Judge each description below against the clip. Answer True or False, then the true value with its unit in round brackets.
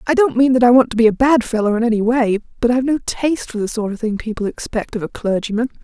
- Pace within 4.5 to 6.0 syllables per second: False (6.7 syllables/s)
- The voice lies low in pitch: False (235 Hz)